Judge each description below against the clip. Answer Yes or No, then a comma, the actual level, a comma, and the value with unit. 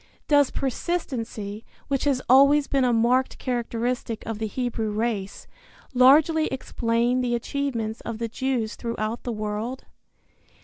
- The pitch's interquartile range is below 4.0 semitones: Yes, average, 2.8 semitones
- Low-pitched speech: No, high, 240 Hz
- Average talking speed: No, slow, 130 wpm